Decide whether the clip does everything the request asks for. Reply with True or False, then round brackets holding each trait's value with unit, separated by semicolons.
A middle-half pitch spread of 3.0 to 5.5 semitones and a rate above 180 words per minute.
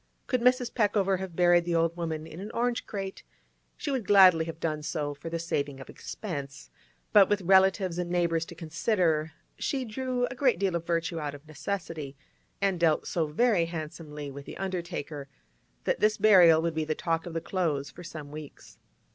True (3.8 semitones; 190 wpm)